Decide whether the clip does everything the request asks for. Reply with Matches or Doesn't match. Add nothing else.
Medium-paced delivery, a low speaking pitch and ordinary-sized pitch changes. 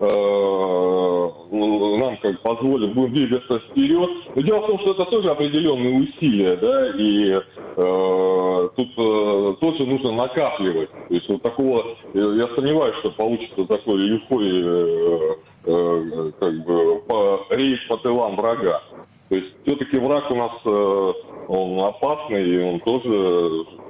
Doesn't match